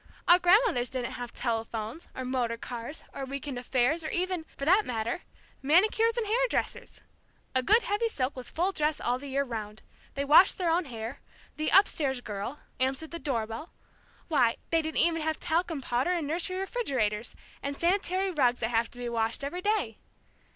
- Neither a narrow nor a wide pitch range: No, wide, 6.4 semitones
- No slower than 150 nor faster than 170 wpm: No, average, 185 wpm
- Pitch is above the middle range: Yes, very high, 280 Hz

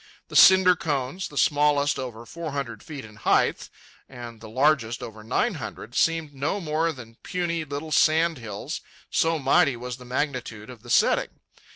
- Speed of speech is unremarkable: Yes, average, 170 wpm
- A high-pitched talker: No, medium, 140 Hz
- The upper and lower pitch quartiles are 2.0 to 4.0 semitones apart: No, average, 5.1 semitones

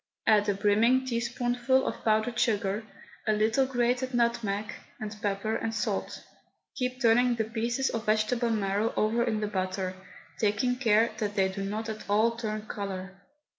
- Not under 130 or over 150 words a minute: No, average, 160 wpm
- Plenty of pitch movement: No, narrow, 2.5 semitones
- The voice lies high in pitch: Yes, high, 220 Hz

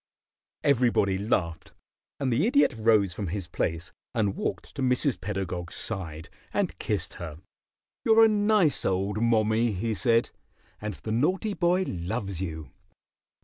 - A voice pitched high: No, low, 110 Hz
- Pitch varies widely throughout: Yes, wide, 5.8 semitones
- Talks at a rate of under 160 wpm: Yes, average, 140 wpm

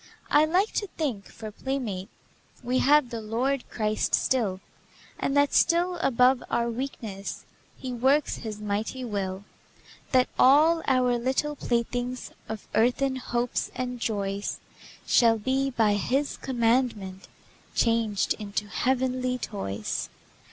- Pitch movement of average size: Yes, average, 3.7 semitones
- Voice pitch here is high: Yes, high, 245 Hz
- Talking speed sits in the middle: No, slow, 125 wpm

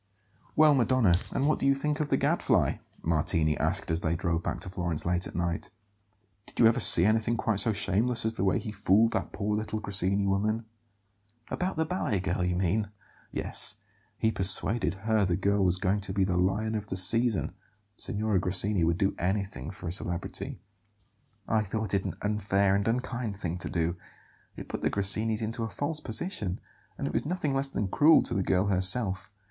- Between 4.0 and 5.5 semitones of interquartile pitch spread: No, average, 3.4 semitones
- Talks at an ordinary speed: Yes, average, 195 wpm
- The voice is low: Yes, low, 100 Hz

